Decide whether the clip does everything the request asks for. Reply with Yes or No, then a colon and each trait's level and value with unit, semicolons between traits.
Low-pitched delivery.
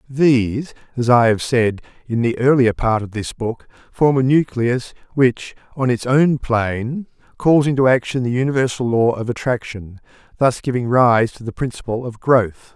Yes: low, 125 Hz